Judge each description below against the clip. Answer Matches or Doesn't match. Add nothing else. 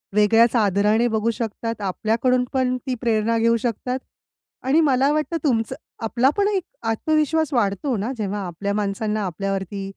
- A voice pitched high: Matches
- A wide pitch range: Doesn't match